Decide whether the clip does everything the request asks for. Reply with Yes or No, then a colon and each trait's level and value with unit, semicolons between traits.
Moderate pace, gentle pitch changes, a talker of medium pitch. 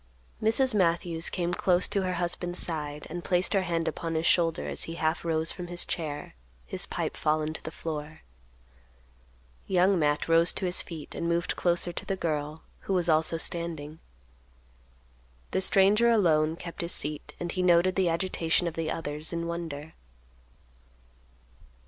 Yes: average, 165 wpm; narrow, 2.0 semitones; medium, 170 Hz